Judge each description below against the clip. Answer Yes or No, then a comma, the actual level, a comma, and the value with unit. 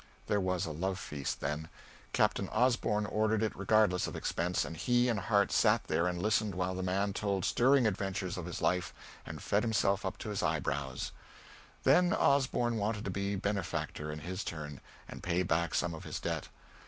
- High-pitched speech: No, very low, 95 Hz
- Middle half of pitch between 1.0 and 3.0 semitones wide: No, average, 3.6 semitones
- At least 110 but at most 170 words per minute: No, average, 190 wpm